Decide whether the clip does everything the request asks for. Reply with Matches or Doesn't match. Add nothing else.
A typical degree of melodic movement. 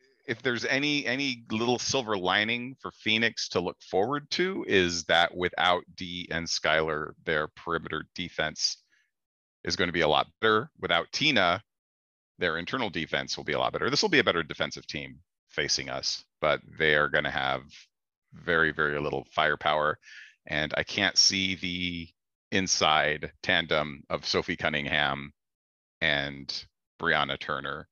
Doesn't match